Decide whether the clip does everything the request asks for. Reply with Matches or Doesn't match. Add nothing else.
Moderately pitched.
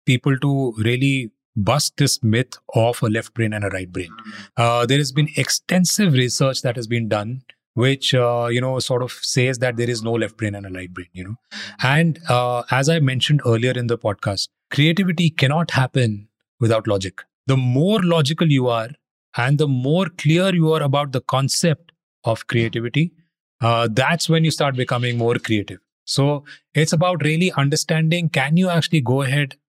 Doesn't match